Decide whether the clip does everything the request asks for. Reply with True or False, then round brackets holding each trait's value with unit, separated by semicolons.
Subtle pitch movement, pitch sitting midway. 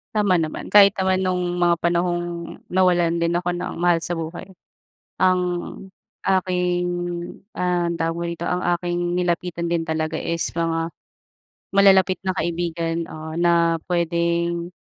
True (1.1 semitones; 175 Hz)